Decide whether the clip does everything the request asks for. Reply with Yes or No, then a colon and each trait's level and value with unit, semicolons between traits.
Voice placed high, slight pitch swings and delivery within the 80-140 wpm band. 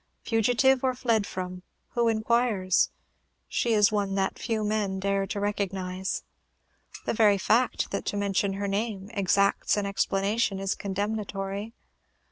Yes: high, 205 Hz; narrow, 2.2 semitones; slow, 135 wpm